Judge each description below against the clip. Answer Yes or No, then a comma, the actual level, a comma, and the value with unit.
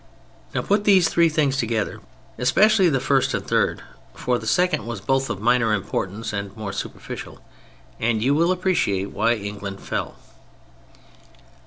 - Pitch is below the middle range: Yes, low, 125 Hz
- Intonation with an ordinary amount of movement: No, wide, 7.5 semitones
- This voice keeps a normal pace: Yes, average, 150 wpm